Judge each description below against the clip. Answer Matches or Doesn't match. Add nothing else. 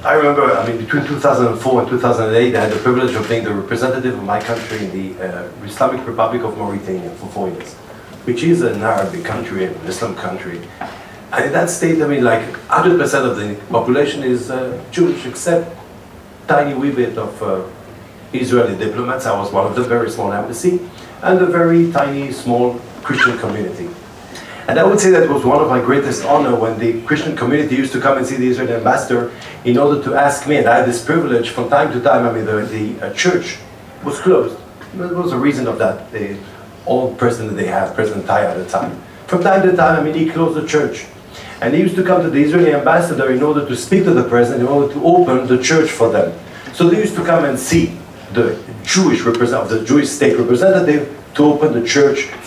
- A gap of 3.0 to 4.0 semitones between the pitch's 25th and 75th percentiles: Doesn't match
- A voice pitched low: Matches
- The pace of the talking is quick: Matches